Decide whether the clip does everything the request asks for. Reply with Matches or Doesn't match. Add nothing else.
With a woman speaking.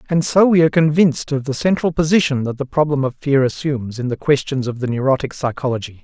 Doesn't match